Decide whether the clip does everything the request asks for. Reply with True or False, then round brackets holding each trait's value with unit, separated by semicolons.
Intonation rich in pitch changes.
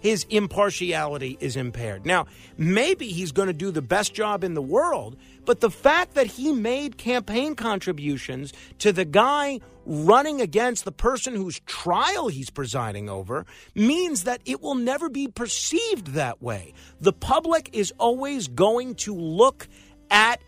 True (8.1 semitones)